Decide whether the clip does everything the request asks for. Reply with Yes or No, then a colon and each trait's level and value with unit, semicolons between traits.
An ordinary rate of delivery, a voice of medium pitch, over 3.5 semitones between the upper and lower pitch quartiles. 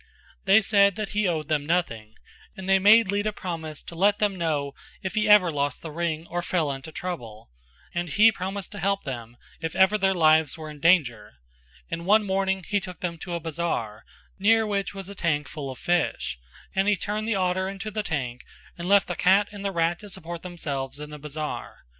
No: fast, 210 wpm; medium, 175 Hz; average, 4.3 semitones